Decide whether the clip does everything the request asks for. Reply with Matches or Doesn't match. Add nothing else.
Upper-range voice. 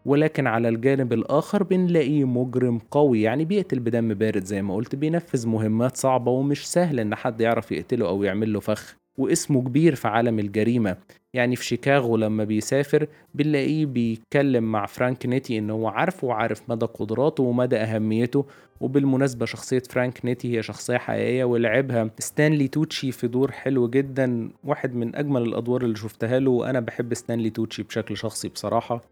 Doesn't match